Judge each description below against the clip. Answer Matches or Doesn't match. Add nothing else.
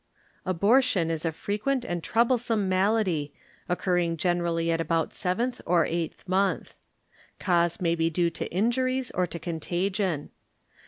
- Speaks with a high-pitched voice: Doesn't match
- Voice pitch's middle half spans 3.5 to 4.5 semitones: Matches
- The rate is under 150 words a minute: Matches